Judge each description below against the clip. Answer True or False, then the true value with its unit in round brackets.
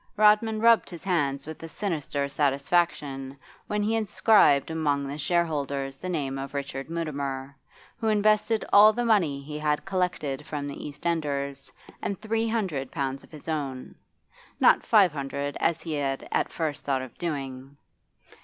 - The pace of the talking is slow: False (160 wpm)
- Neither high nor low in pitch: True (150 Hz)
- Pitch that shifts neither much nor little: True (4.9 semitones)